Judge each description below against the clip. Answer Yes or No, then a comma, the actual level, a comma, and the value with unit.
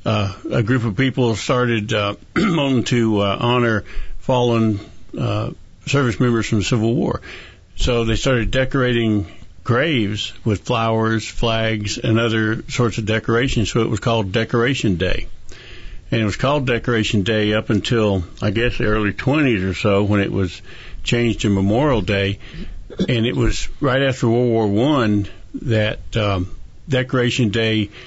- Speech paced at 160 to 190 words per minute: No, average, 150 wpm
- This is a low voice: Yes, low, 110 Hz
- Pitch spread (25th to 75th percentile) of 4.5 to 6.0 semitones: No, average, 2.8 semitones